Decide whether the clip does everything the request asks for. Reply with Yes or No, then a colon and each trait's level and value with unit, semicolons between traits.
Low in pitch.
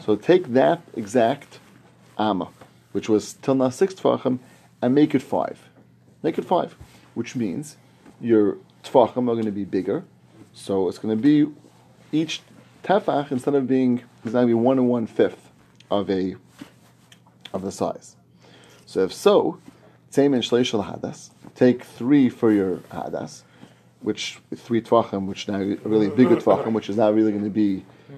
Yes: low, 115 Hz